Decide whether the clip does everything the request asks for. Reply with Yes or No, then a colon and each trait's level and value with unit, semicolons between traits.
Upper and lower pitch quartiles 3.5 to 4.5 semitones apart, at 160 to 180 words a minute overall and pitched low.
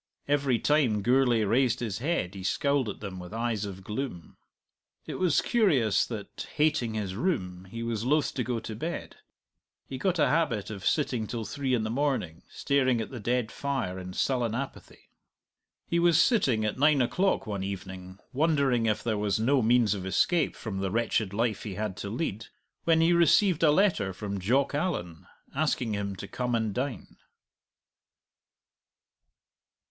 No: wide, 5.5 semitones; average, 170 wpm; low, 120 Hz